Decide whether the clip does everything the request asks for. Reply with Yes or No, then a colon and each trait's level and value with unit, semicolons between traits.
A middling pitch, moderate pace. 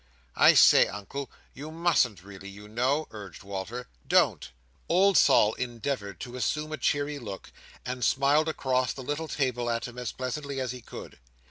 No: low, 125 Hz; average, 165 wpm